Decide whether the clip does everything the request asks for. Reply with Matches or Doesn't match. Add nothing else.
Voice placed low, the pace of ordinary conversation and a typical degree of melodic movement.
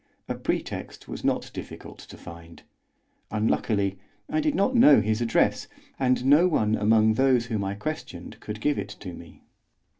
Matches